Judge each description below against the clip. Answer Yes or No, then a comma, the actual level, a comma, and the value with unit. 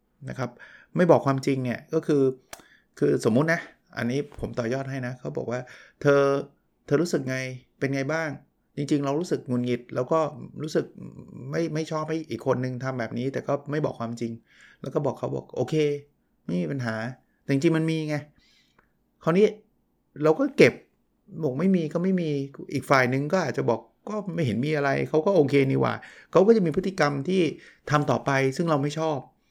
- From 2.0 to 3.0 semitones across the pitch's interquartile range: No, average, 3.6 semitones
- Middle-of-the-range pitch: Yes, medium, 145 Hz